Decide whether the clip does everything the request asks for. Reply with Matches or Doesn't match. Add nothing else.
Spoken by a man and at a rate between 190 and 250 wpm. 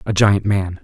Matches